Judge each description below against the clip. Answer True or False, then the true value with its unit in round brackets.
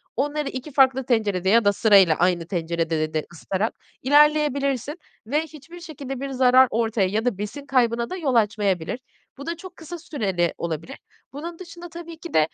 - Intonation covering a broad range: True (7.3 semitones)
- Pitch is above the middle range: True (250 Hz)